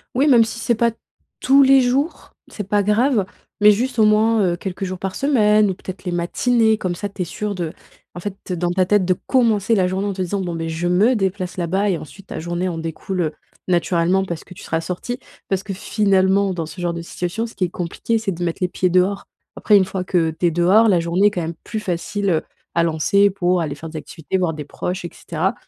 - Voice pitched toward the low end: No, high, 190 Hz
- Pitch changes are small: No, average, 3.3 semitones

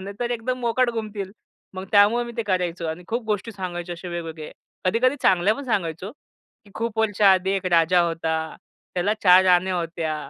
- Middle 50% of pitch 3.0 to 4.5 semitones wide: Yes, average, 4.1 semitones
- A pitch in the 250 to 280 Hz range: No, high, 190 Hz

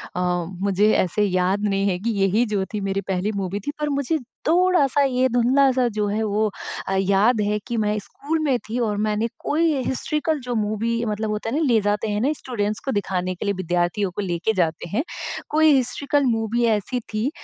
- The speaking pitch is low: No, high, 215 Hz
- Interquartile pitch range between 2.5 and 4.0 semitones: No, average, 4.4 semitones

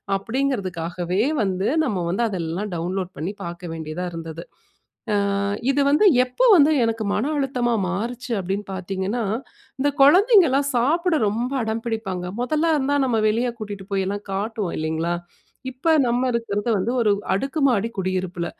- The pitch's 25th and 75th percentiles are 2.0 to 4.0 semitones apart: No, wide, 5.5 semitones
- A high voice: Yes, high, 210 Hz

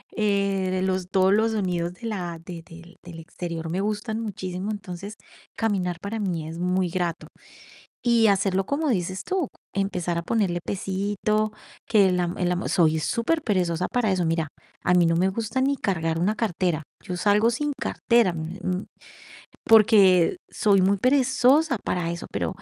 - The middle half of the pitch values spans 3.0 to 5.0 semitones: Yes, average, 3.5 semitones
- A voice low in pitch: No, high, 190 Hz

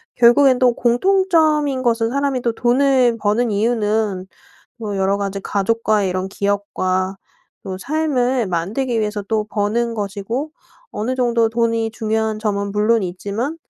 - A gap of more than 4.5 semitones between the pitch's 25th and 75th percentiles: No, average, 3.4 semitones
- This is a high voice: Yes, high, 225 Hz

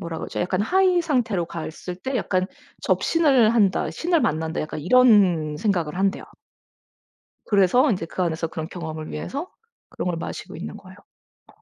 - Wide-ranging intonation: Yes, wide, 7.2 semitones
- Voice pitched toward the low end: No, medium, 185 Hz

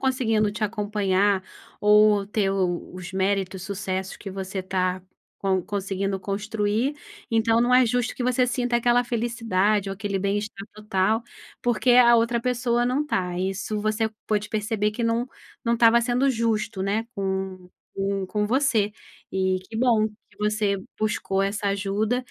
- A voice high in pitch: Yes, high, 210 Hz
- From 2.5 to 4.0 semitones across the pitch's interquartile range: Yes, average, 3.0 semitones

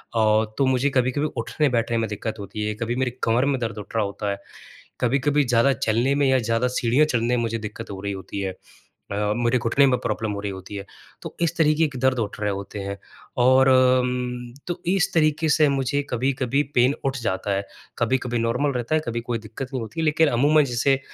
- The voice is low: Yes, low, 125 Hz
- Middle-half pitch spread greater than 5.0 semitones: No, average, 3.6 semitones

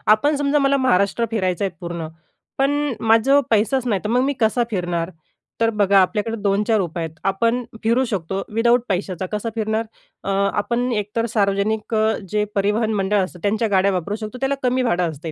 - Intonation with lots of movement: No, average, 3.1 semitones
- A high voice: Yes, high, 210 Hz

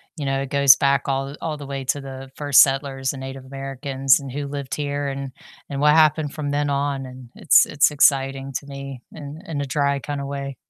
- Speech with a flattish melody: Yes, narrow, 1.0 semitones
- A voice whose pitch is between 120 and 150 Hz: Yes, medium, 140 Hz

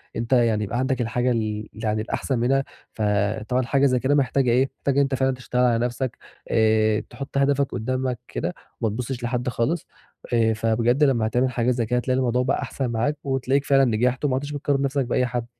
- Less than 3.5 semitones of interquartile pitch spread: Yes, narrow, 2.6 semitones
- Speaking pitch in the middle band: No, low, 125 Hz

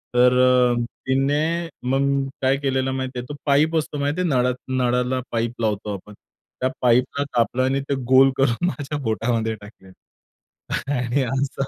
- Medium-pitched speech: No, low, 130 Hz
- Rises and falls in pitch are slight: Yes, narrow, 2.3 semitones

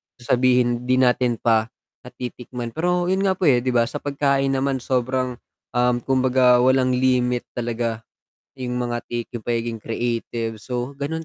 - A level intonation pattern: Yes, narrow, 1.6 semitones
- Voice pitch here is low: Yes, low, 125 Hz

